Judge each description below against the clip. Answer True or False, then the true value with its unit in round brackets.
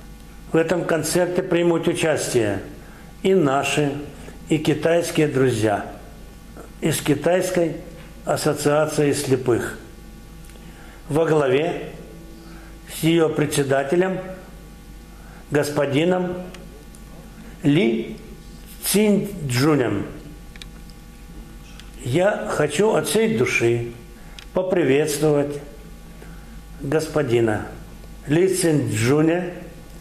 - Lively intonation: False (3.2 semitones)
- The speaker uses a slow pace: True (60 wpm)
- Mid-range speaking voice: True (155 Hz)